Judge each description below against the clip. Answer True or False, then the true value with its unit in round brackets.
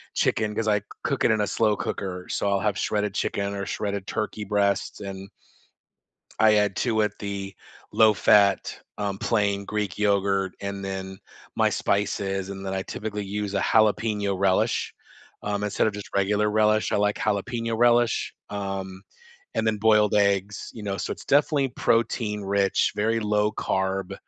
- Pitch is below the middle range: True (105 Hz)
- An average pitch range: False (1.4 semitones)